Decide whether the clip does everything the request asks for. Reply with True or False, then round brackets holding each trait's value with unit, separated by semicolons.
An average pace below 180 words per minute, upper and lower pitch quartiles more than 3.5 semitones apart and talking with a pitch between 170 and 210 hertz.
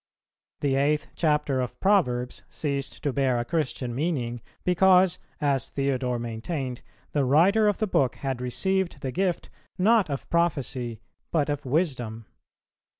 False (140 wpm; 5.4 semitones; 140 Hz)